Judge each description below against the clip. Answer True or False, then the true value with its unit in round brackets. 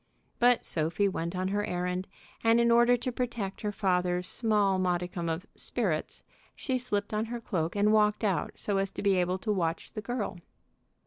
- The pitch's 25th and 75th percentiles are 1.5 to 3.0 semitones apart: False (3.9 semitones)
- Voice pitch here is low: False (200 Hz)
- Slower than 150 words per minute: False (185 wpm)